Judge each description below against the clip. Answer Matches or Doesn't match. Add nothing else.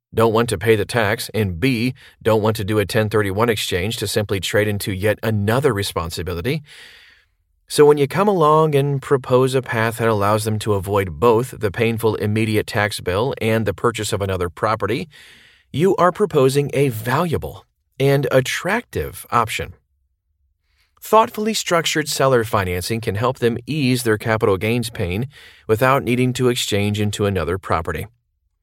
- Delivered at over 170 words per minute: Doesn't match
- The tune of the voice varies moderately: Matches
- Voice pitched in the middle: Doesn't match